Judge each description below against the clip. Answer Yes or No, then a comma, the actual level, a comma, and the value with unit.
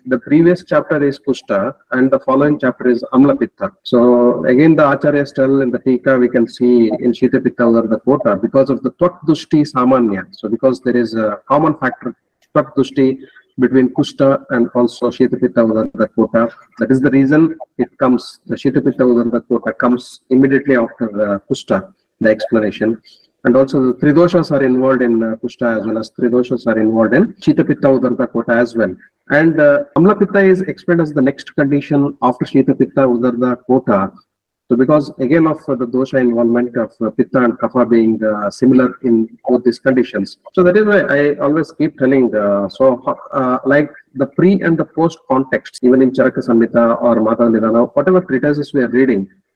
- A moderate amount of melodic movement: Yes, average, 3.3 semitones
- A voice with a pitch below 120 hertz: No, low, 130 Hz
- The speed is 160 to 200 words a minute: Yes, average, 180 wpm